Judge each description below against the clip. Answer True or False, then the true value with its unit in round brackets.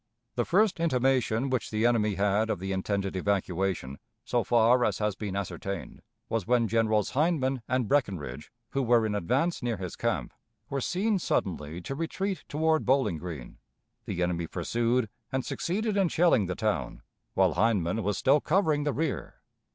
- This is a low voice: True (115 Hz)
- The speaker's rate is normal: True (165 wpm)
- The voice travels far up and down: True (6.1 semitones)